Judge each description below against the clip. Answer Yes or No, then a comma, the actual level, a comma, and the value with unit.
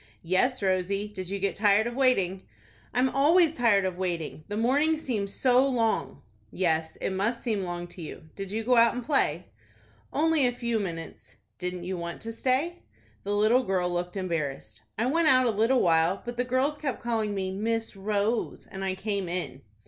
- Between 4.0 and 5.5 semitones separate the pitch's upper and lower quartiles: Yes, average, 5.1 semitones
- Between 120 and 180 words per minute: No, average, 190 wpm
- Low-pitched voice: No, high, 210 Hz